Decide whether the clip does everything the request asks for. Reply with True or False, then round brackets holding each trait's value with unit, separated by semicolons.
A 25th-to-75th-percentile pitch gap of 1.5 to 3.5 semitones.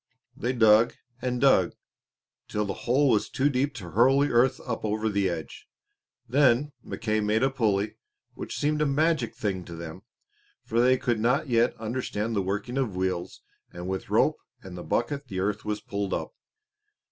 False (4.4 semitones)